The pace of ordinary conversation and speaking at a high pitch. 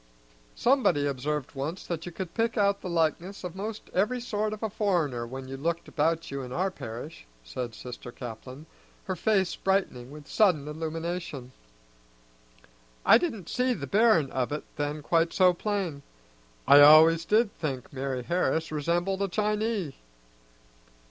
No: average, 155 wpm; medium, 165 Hz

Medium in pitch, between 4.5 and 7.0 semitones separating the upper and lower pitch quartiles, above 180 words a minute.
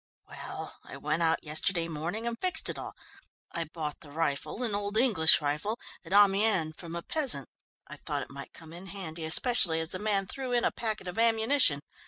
Yes: medium, 180 Hz; wide, 5.6 semitones; average, 200 wpm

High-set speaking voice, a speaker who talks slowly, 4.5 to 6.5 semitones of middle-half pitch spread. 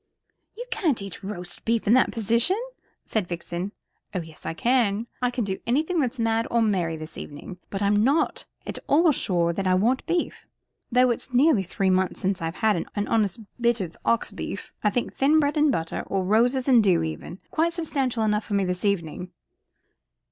No: high, 215 Hz; average, 200 wpm; average, 5.3 semitones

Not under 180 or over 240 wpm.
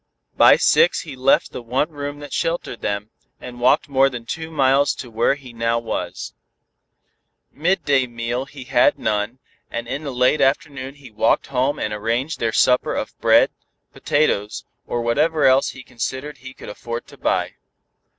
No: average, 170 wpm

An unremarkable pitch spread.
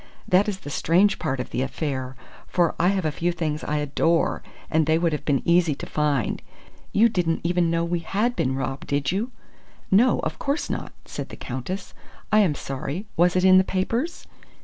Yes: average, 4.4 semitones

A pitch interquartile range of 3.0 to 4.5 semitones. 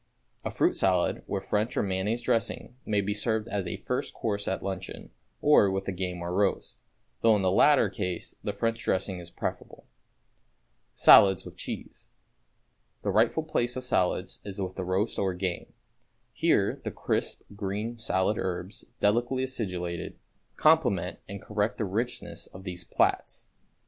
Yes: average, 3.4 semitones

